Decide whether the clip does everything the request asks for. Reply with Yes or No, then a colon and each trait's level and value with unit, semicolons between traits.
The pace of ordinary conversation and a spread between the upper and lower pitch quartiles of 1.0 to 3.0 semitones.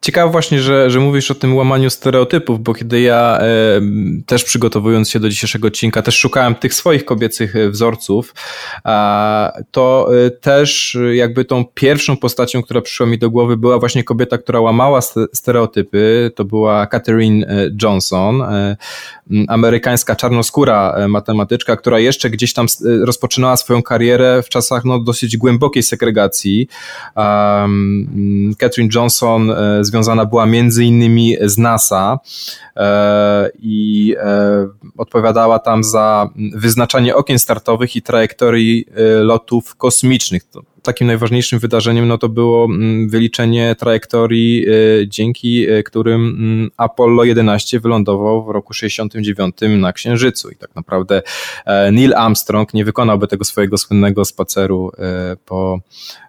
Yes: average, 125 wpm; narrow, 2.5 semitones